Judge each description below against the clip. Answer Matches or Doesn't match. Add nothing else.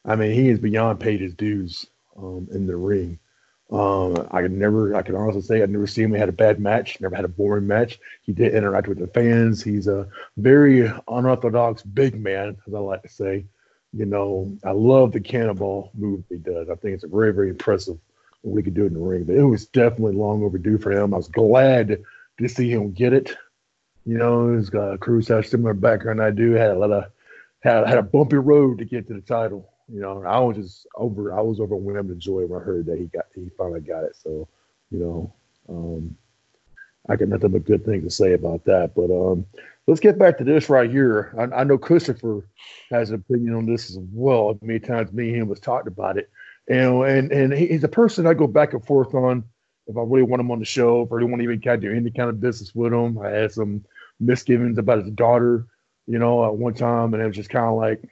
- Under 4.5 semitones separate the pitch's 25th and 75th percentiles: Matches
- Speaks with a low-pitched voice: Matches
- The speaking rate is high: Matches